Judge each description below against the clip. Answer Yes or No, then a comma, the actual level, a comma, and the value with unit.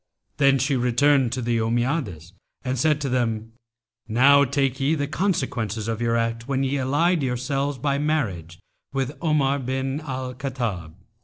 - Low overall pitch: Yes, low, 130 Hz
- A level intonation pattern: No, average, 3.3 semitones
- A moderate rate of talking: Yes, average, 155 wpm